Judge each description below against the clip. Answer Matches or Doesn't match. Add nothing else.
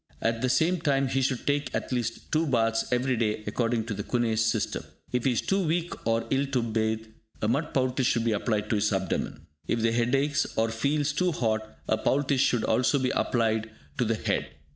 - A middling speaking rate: Doesn't match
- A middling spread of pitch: Matches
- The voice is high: Doesn't match